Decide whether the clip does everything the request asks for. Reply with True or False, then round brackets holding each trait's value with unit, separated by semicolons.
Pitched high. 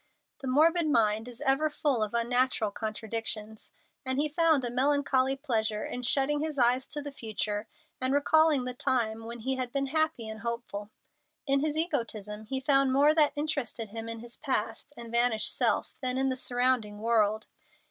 True (250 Hz)